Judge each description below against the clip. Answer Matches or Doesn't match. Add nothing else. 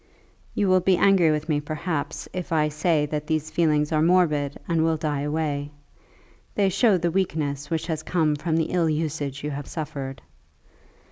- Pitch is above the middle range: Doesn't match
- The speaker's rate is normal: Matches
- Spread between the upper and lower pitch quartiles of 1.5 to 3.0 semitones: Matches